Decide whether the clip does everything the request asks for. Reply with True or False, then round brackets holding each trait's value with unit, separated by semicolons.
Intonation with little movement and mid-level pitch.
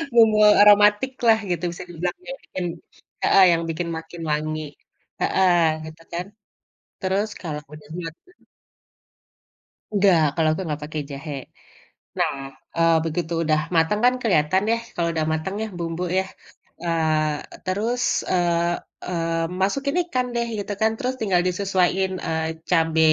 False (3.8 semitones; 175 Hz)